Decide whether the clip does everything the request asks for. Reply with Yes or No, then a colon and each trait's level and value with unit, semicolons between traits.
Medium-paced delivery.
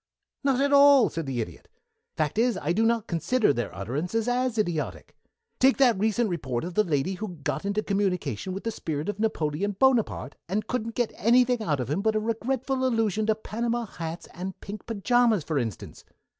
Yes: average, 190 wpm